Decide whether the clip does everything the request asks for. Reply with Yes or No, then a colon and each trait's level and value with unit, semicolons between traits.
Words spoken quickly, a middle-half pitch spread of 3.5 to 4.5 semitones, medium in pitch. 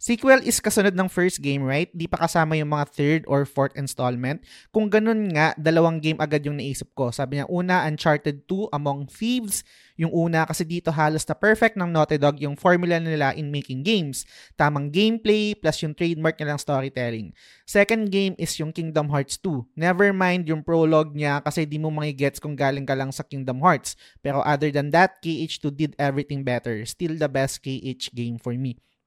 Yes: fast, 195 wpm; average, 3.8 semitones; medium, 155 Hz